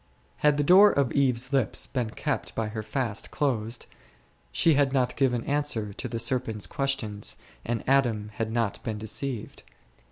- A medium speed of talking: Yes, average, 160 wpm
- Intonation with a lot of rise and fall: No, average, 3.9 semitones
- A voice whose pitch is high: No, low, 120 Hz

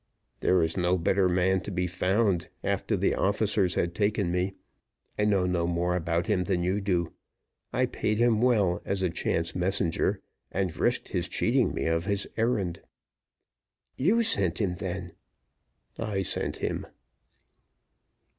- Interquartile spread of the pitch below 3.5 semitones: Yes, narrow, 2.5 semitones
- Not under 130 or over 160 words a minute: Yes, average, 150 wpm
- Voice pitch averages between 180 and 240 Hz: No, very low, 95 Hz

